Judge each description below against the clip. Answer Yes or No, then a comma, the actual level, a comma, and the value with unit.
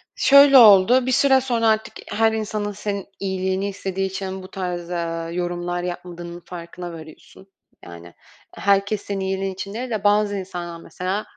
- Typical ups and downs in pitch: Yes, average, 3.0 semitones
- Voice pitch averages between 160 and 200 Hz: Yes, high, 190 Hz